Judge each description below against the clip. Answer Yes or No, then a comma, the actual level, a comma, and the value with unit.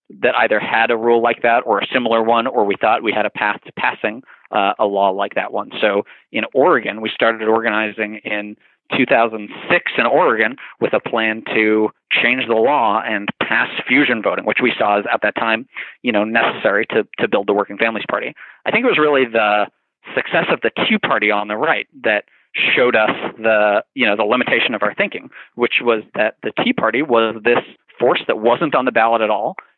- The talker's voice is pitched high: No, low, 110 Hz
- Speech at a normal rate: No, fast, 210 wpm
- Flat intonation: Yes, narrow, 1.6 semitones